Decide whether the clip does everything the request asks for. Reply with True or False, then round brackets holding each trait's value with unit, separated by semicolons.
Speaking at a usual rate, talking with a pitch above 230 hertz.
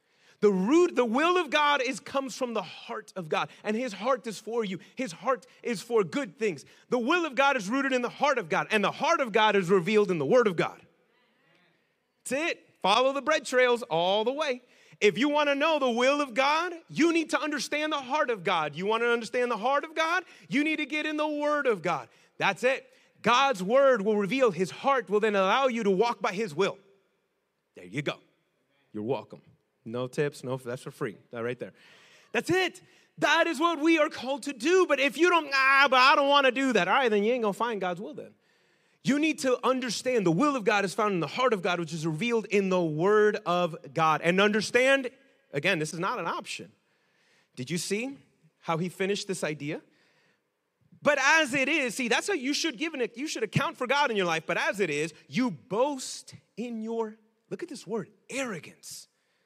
False (225 wpm; 240 Hz)